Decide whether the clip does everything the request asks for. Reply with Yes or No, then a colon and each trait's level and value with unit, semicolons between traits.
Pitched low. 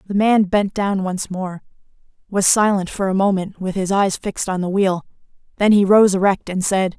No: high, 195 Hz